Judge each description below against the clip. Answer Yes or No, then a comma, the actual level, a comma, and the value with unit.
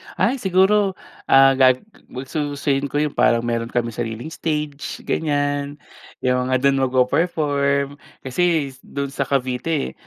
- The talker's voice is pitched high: No, medium, 140 Hz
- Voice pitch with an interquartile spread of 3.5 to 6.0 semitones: No, average, 2.8 semitones